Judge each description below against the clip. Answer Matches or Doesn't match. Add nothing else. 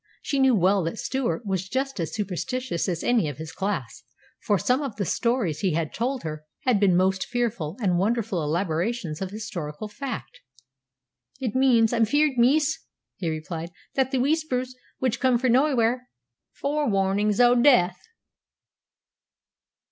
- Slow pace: Doesn't match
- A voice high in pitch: Matches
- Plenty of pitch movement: Matches